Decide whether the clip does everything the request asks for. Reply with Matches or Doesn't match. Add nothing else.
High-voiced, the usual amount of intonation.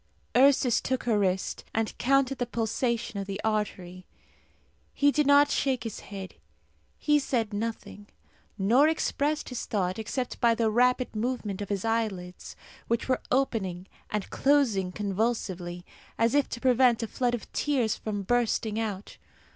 Matches